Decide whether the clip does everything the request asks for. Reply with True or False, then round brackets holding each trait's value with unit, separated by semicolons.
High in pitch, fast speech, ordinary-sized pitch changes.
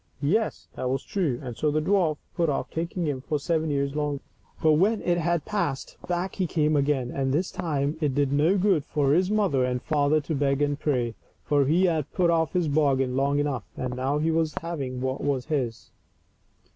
False (150 Hz; 210 wpm; 3.4 semitones)